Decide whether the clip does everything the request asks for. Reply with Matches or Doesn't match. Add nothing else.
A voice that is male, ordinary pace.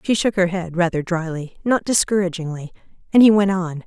Doesn't match